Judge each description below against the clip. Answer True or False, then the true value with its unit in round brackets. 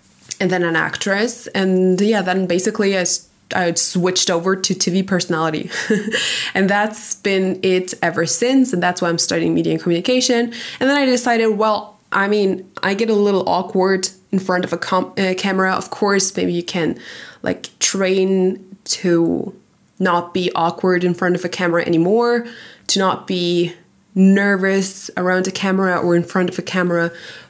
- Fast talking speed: False (170 wpm)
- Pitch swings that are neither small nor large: False (2.2 semitones)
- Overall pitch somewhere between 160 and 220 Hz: True (190 Hz)